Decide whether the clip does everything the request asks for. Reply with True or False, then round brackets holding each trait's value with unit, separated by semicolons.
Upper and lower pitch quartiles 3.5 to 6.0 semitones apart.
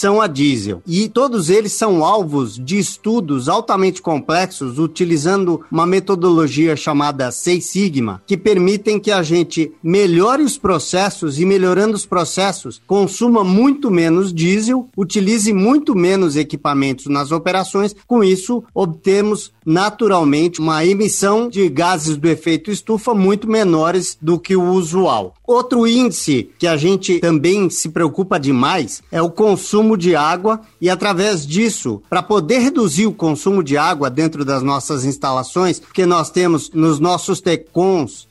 True (4.2 semitones)